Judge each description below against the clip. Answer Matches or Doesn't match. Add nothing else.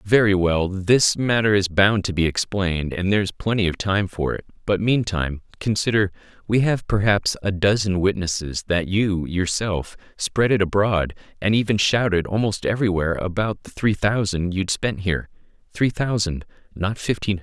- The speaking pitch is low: Matches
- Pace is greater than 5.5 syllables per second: Doesn't match